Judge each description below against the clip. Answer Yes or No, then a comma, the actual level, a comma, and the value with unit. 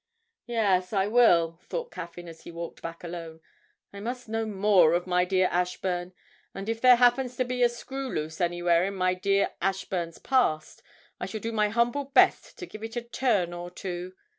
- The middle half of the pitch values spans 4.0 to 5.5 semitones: Yes, average, 5.2 semitones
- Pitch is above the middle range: Yes, high, 195 Hz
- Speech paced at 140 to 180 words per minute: No, average, 190 wpm